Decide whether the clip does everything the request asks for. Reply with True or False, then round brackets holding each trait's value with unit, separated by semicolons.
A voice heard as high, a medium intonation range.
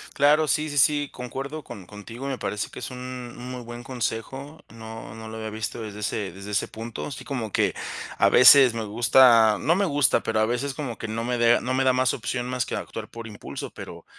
False (120 Hz; 3.1 semitones)